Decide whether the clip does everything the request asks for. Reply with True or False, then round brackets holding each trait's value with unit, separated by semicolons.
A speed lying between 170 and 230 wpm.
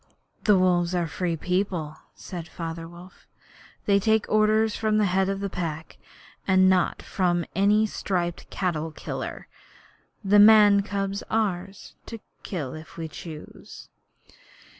False (140 wpm)